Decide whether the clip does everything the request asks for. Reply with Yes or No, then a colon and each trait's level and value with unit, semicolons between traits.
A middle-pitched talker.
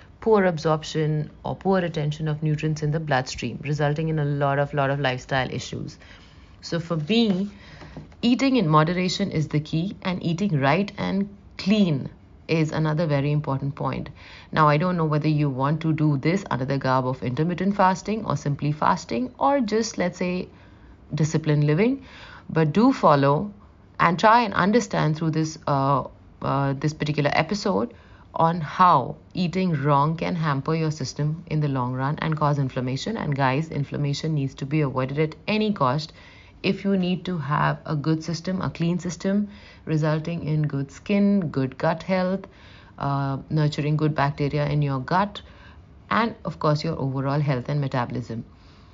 Yes: medium, 155 Hz